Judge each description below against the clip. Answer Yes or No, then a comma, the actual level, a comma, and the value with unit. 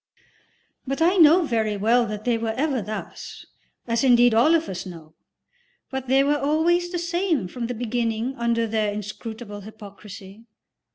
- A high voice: Yes, high, 235 Hz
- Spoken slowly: No, average, 155 wpm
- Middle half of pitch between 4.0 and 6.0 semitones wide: Yes, average, 4.6 semitones